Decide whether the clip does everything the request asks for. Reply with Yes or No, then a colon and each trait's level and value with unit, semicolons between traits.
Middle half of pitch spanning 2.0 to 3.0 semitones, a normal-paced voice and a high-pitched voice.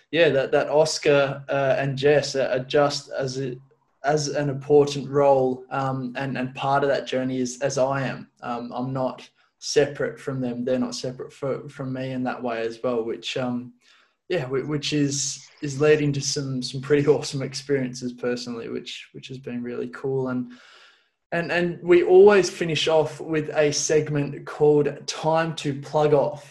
No: narrow, 2.4 semitones; average, 175 wpm; medium, 140 Hz